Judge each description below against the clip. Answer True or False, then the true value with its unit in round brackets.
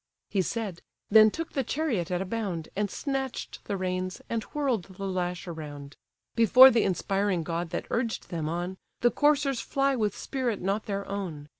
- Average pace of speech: True (175 wpm)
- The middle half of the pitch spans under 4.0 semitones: False (4.8 semitones)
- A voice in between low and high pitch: False (200 Hz)